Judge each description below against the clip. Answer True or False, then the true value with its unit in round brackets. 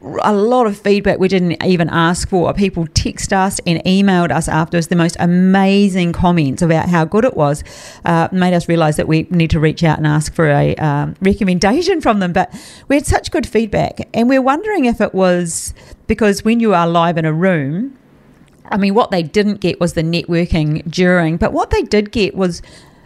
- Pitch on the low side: False (180 Hz)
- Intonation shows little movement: False (3.7 semitones)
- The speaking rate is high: True (210 wpm)